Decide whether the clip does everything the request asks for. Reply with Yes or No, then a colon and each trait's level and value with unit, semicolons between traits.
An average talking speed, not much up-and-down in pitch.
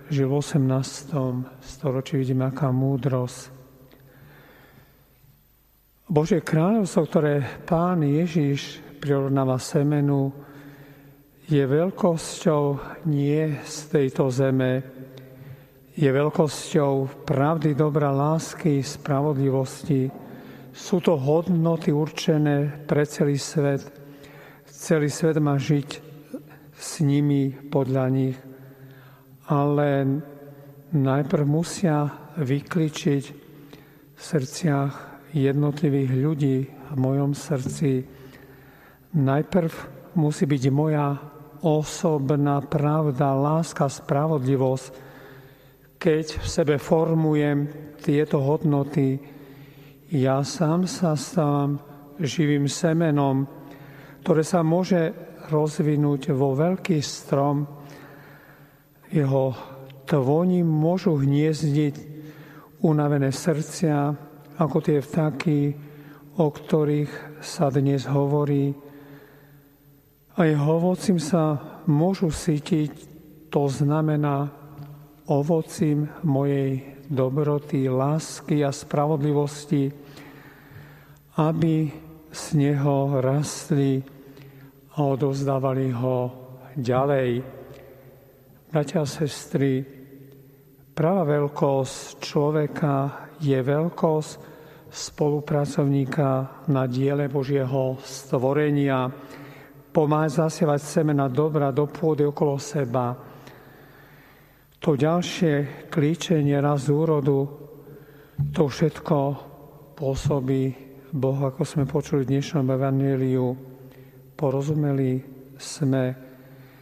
No: slow, 80 wpm; narrow, 1.9 semitones